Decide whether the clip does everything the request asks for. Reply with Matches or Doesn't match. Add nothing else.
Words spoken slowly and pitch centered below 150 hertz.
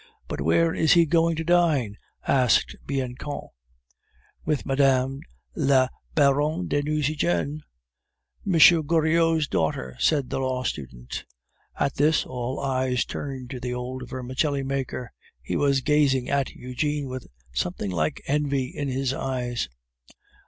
Matches